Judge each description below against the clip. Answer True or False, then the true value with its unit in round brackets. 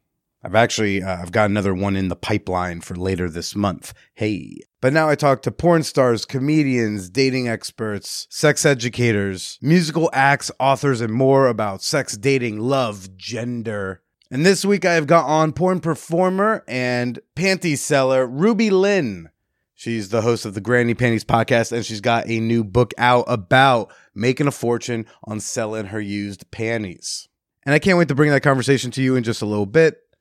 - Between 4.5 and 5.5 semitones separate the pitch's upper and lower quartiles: True (5.0 semitones)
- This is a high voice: False (120 Hz)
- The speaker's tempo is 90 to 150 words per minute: False (180 wpm)